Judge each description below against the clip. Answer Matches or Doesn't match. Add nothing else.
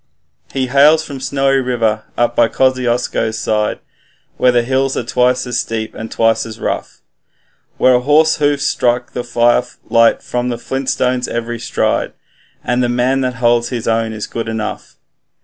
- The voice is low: Matches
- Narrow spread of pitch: Matches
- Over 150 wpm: Matches